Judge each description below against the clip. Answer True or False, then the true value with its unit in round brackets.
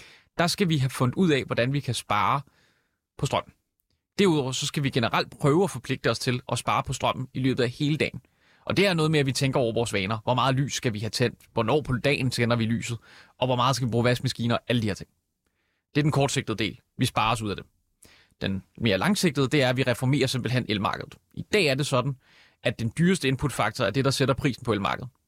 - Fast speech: True (245 wpm)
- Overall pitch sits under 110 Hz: False (125 Hz)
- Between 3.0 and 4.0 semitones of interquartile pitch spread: True (3.5 semitones)